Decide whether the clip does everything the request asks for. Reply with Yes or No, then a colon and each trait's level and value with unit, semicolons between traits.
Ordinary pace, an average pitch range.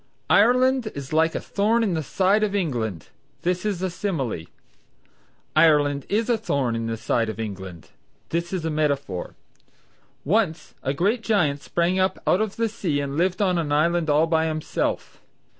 No: average, 165 wpm; wide, 6.0 semitones